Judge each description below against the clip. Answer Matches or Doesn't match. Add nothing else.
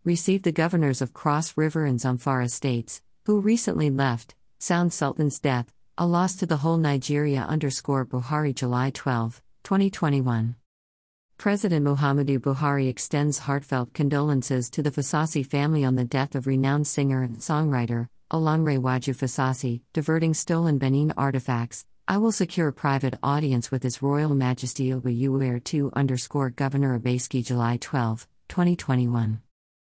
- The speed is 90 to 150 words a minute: Matches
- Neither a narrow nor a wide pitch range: Matches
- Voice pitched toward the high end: Doesn't match